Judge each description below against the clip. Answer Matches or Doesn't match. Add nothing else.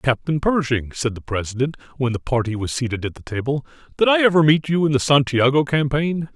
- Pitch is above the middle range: Doesn't match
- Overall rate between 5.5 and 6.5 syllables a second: Matches